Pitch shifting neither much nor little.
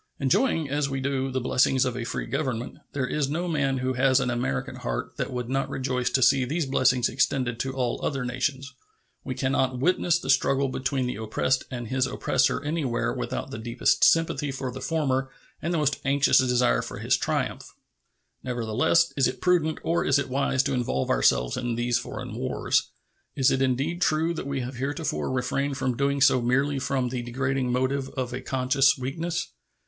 No: narrow, 1.9 semitones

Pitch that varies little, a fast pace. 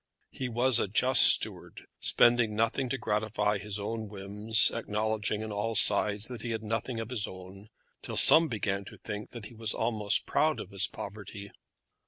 No: narrow, 2.0 semitones; average, 180 wpm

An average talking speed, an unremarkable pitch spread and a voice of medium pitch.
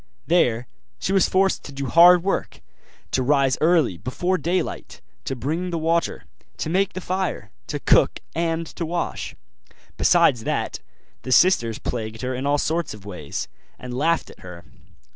No: average, 160 wpm; wide, 5.8 semitones; medium, 155 Hz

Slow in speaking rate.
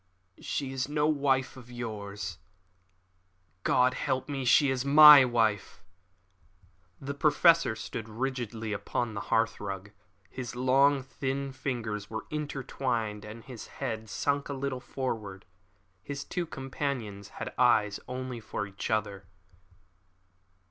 Yes: slow, 120 wpm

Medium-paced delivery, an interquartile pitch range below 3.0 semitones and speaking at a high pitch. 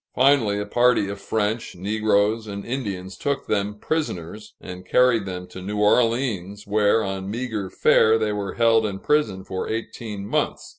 No: average, 160 wpm; narrow, 2.6 semitones; low, 105 Hz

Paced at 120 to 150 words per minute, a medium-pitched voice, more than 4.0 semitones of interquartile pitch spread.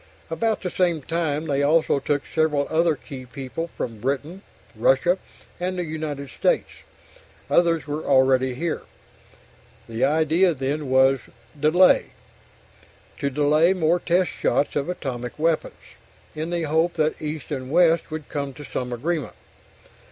No: average, 140 wpm; medium, 155 Hz; average, 3.3 semitones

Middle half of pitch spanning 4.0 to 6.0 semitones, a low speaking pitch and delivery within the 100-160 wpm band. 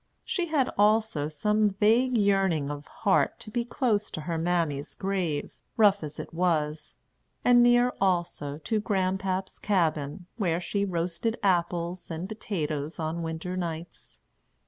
No: average, 4.5 semitones; medium, 180 Hz; average, 140 wpm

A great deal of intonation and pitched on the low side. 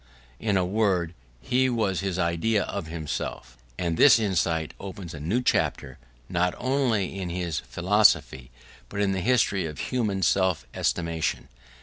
No: average, 3.7 semitones; very low, 95 Hz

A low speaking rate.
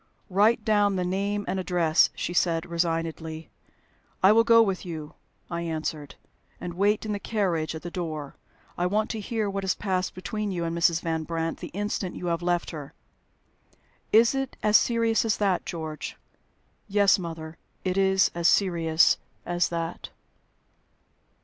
No: average, 160 wpm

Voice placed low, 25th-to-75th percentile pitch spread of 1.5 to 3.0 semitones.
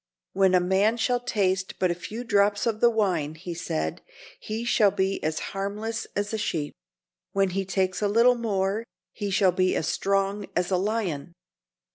No: high, 195 Hz; average, 2.7 semitones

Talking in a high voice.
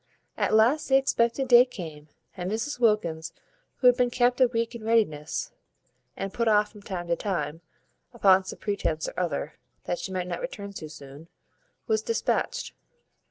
Yes: high, 210 Hz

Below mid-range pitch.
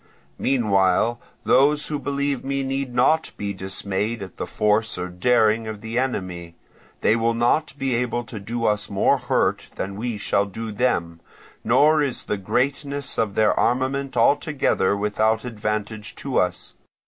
Yes: low, 115 Hz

